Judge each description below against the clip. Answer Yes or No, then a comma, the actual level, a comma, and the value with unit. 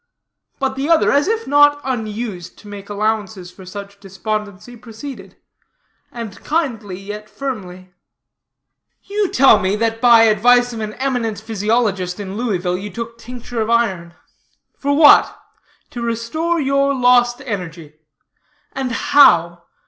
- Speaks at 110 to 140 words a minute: Yes, slow, 135 wpm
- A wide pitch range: No, average, 4.1 semitones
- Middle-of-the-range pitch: No, high, 225 Hz